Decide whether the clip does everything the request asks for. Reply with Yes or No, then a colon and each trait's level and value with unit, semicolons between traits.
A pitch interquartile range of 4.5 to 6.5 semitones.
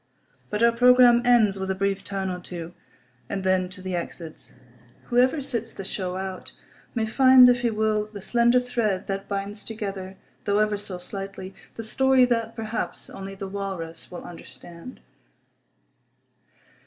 No: average, 3.7 semitones